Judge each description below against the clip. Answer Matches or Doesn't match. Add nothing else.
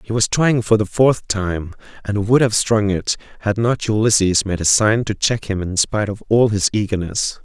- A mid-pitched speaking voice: Doesn't match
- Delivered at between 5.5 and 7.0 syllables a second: Doesn't match